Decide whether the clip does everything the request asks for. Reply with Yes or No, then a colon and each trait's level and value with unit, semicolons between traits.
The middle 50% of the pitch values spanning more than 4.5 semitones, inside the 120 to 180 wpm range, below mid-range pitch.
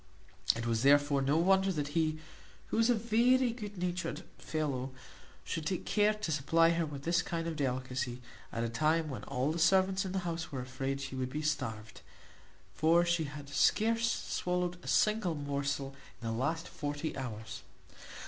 No: average, 4.9 semitones; average, 175 wpm; medium, 155 Hz